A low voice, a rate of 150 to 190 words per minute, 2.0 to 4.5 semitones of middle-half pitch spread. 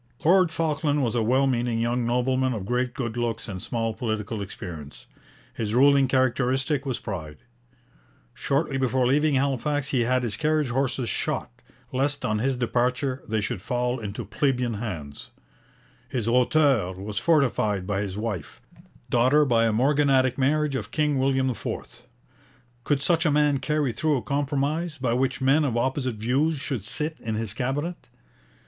Yes: low, 130 Hz; average, 160 wpm; average, 3.7 semitones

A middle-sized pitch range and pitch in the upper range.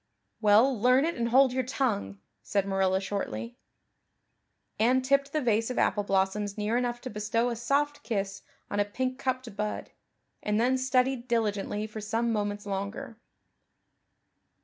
Yes: average, 3.9 semitones; high, 225 Hz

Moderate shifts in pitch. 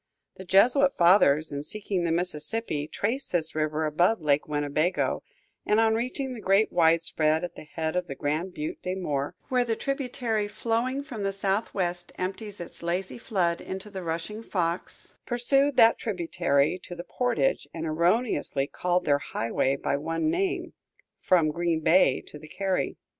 No: wide, 5.7 semitones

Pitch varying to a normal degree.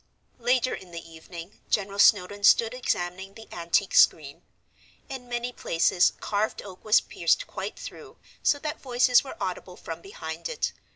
No: wide, 5.7 semitones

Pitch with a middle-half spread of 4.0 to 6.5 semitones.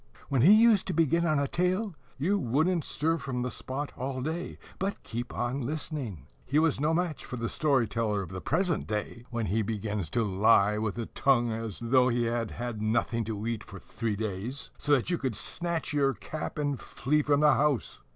Yes: wide, 5.4 semitones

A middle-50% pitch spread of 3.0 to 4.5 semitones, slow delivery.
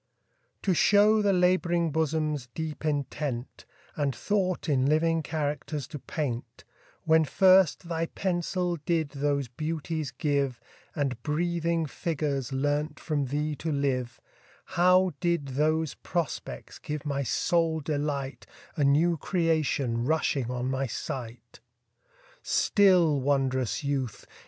Yes: average, 3.3 semitones; slow, 120 wpm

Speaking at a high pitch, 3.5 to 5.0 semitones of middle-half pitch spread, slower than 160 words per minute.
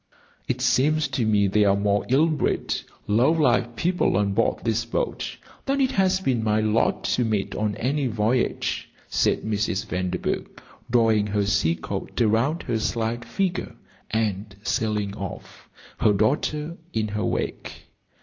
No: low, 115 Hz; average, 3.9 semitones; average, 150 wpm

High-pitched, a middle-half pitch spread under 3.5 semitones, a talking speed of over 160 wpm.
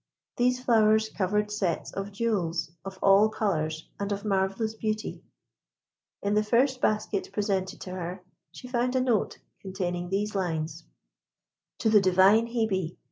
No: high, 205 Hz; average, 2.7 semitones; average, 140 wpm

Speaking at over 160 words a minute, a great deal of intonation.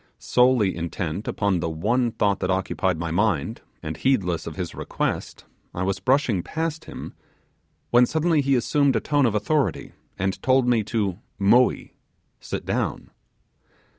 No: average, 150 wpm; wide, 5.9 semitones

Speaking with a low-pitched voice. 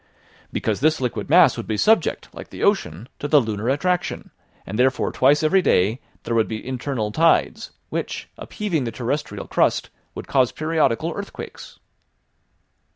Yes: low, 130 Hz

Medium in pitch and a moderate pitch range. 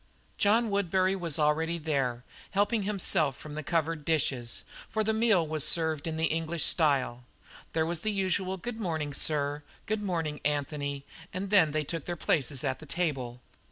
Yes: medium, 160 Hz; average, 4.2 semitones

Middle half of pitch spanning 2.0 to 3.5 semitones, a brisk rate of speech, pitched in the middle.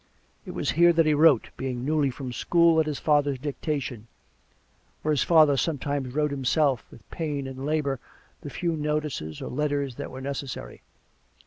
No: narrow, 2.5 semitones; average, 175 wpm; medium, 145 Hz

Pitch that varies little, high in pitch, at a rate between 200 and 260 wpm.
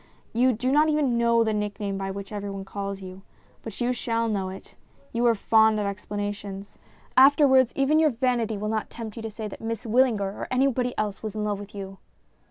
No: average, 3.3 semitones; high, 220 Hz; fast, 205 wpm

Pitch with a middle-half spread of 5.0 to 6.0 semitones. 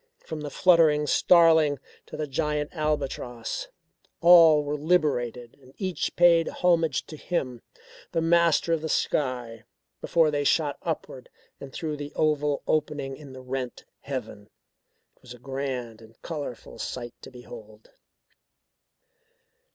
No: average, 4.0 semitones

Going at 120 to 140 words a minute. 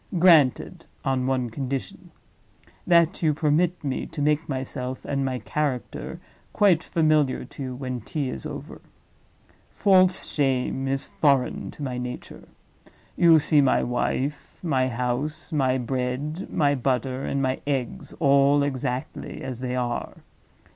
Yes: slow, 135 wpm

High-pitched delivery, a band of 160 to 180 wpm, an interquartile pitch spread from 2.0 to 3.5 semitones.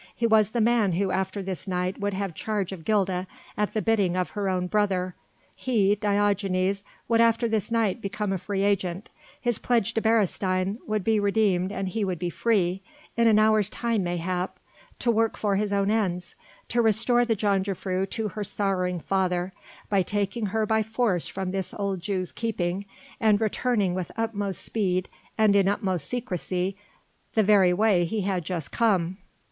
Yes: high, 200 Hz; average, 175 wpm; average, 2.8 semitones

